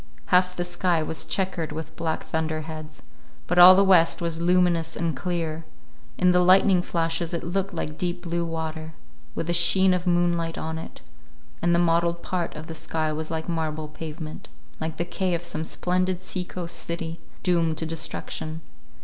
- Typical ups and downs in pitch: No, narrow, 1.8 semitones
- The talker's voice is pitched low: No, medium, 170 Hz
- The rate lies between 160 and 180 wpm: Yes, average, 175 wpm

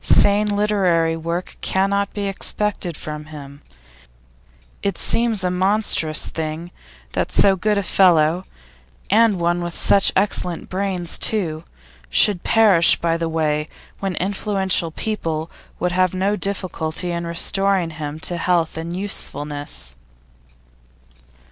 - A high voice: No, medium, 180 Hz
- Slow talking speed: Yes, slow, 125 wpm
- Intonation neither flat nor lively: Yes, average, 3.5 semitones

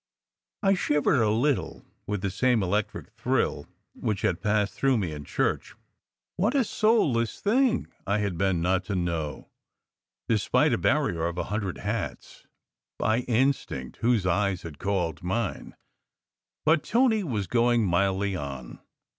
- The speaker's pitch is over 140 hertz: No, low, 105 Hz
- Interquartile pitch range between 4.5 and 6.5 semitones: Yes, wide, 5.5 semitones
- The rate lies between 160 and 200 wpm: No, average, 145 wpm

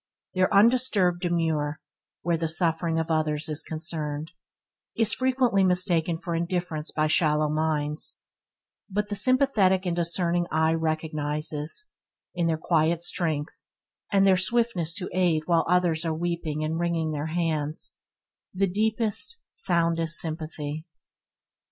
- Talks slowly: Yes, slow, 125 wpm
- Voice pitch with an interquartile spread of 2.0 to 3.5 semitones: Yes, average, 2.8 semitones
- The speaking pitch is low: No, medium, 165 Hz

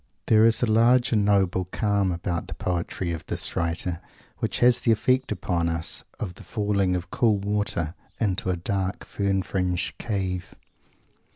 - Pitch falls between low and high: No, very low, 95 Hz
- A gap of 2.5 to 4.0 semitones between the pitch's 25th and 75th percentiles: Yes, average, 3.2 semitones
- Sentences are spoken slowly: No, average, 165 wpm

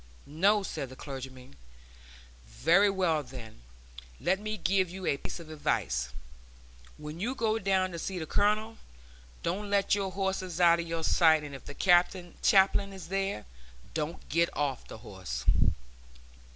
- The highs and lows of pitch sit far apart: No, average, 5.0 semitones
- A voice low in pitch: No, medium, 175 Hz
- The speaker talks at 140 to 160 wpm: Yes, average, 150 wpm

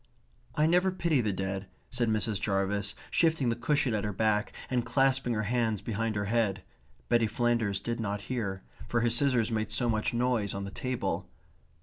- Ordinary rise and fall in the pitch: Yes, average, 3.3 semitones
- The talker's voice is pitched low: Yes, low, 115 Hz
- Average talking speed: Yes, average, 185 wpm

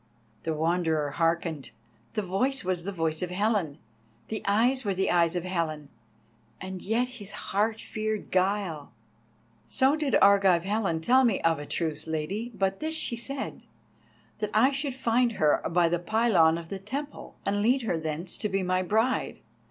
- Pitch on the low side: No, high, 195 Hz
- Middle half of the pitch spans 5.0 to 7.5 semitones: Yes, average, 5.3 semitones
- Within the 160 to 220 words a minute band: Yes, average, 170 wpm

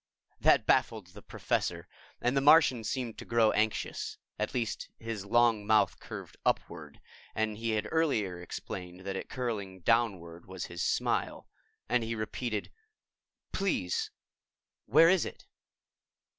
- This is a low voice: Yes, low, 110 Hz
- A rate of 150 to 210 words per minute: No, slow, 135 wpm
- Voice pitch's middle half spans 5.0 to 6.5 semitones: No, average, 3.7 semitones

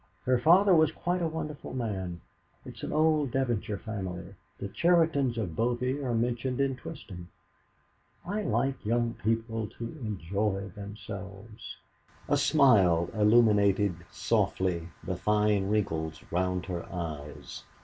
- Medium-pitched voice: No, low, 110 Hz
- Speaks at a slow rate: Yes, slow, 125 wpm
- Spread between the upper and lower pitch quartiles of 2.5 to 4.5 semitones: No, wide, 5.4 semitones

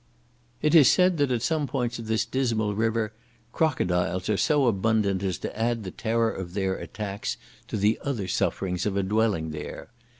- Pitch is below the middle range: Yes, low, 110 Hz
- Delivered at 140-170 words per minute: No, average, 180 wpm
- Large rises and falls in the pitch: No, average, 3.9 semitones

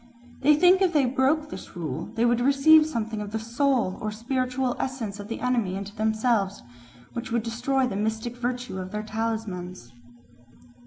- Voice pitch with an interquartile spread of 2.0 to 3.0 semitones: No, average, 3.7 semitones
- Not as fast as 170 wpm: No, average, 175 wpm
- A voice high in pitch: Yes, high, 235 Hz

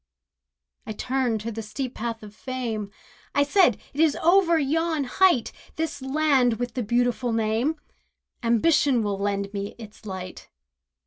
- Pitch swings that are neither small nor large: Yes, average, 4.9 semitones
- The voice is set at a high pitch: Yes, high, 245 Hz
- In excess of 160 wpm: No, average, 145 wpm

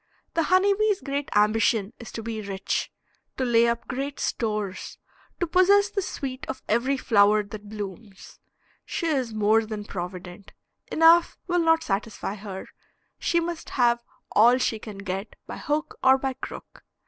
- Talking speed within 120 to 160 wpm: Yes, average, 155 wpm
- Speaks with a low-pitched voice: No, high, 235 Hz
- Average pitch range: No, wide, 6.3 semitones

